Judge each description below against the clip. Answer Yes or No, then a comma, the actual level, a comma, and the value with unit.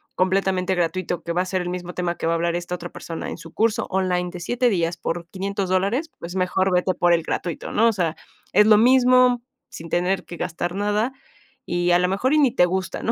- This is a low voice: No, medium, 185 Hz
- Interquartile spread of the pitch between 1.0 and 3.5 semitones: Yes, average, 2.8 semitones